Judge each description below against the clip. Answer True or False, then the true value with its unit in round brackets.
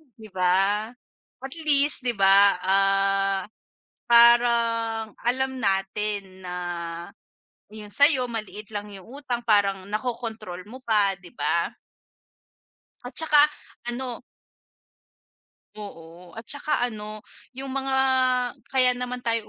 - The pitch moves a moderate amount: True (4.0 semitones)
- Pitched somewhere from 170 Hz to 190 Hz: False (220 Hz)